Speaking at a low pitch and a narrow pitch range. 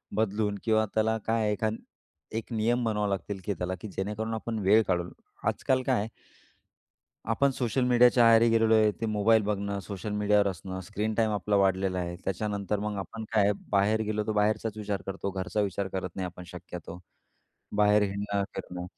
Yes: low, 105 Hz; narrow, 2.2 semitones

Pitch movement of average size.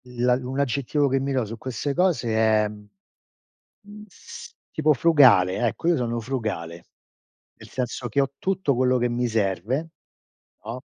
Yes: average, 3.9 semitones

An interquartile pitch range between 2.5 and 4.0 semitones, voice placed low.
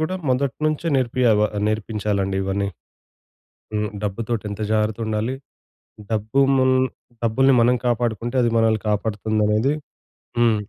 Yes: average, 2.8 semitones; low, 110 Hz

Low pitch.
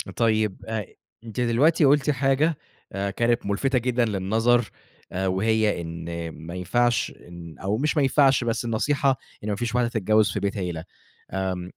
Yes: low, 110 Hz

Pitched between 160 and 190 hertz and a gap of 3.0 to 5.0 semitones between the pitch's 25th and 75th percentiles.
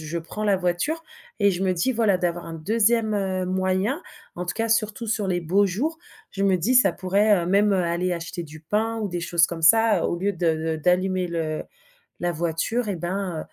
Yes: medium, 185 Hz; average, 3.6 semitones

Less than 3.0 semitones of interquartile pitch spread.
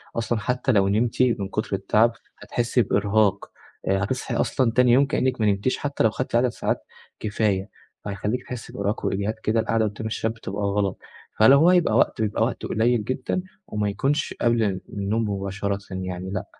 No: average, 3.3 semitones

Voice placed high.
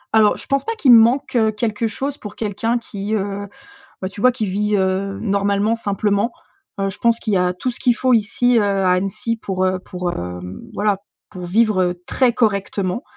Yes: high, 205 Hz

